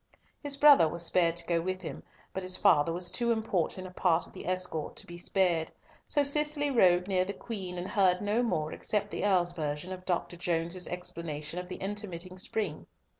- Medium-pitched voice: Yes, medium, 180 Hz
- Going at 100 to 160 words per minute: No, average, 200 wpm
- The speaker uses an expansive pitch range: No, average, 3.0 semitones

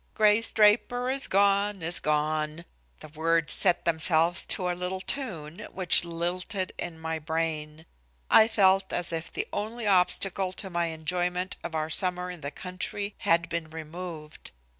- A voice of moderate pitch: Yes, medium, 175 Hz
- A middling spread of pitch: Yes, average, 3.0 semitones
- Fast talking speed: No, average, 155 wpm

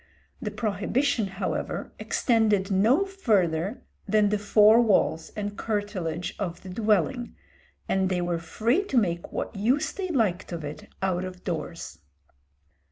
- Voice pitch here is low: No, high, 205 Hz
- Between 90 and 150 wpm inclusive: Yes, average, 140 wpm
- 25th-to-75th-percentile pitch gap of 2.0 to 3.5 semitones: No, average, 3.9 semitones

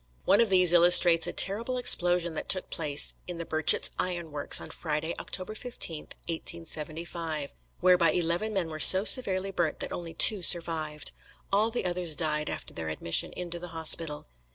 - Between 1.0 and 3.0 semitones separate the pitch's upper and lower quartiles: Yes, narrow, 2.5 semitones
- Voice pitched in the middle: Yes, medium, 170 Hz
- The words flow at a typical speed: Yes, average, 170 wpm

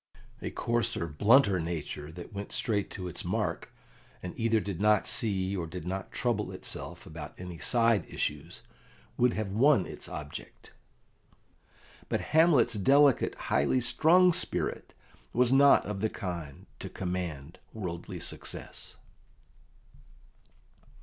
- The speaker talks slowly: Yes, slow, 125 wpm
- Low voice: Yes, low, 100 Hz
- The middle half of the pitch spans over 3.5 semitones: Yes, average, 5.3 semitones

